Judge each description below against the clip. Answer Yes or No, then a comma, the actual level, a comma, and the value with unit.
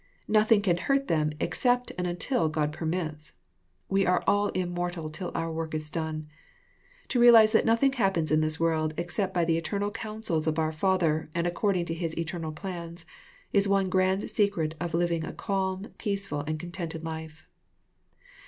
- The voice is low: No, medium, 175 Hz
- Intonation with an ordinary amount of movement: Yes, average, 3.8 semitones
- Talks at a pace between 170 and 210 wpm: Yes, average, 175 wpm